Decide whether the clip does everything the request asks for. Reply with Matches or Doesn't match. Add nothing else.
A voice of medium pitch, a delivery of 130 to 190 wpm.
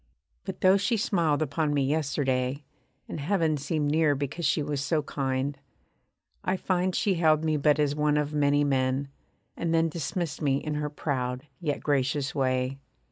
Matches